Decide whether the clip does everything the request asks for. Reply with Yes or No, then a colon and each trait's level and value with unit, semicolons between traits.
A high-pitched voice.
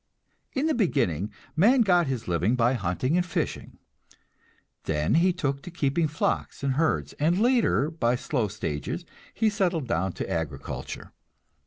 No: medium, 140 Hz